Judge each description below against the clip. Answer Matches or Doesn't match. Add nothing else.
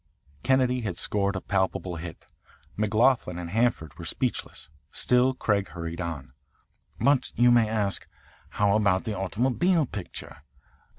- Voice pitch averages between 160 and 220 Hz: Doesn't match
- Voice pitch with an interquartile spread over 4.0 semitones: Matches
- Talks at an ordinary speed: Doesn't match